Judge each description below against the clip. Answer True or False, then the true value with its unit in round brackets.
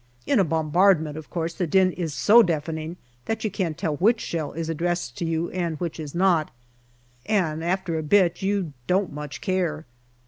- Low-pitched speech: False (170 Hz)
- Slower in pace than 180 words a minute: False (185 wpm)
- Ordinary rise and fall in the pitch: True (3.0 semitones)